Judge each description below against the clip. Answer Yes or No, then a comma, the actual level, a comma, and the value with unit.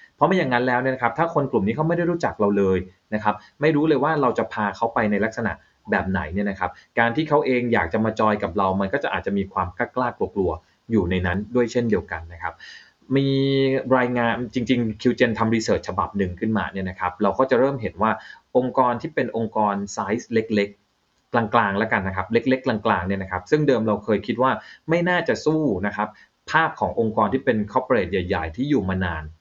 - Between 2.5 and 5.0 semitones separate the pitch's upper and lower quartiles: Yes, average, 4.6 semitones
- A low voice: Yes, low, 110 Hz